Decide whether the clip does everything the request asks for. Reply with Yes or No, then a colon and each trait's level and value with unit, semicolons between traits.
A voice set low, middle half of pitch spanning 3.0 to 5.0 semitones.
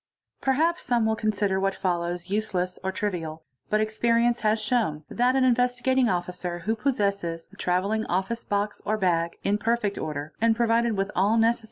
No: high, 210 Hz; average, 4.4 semitones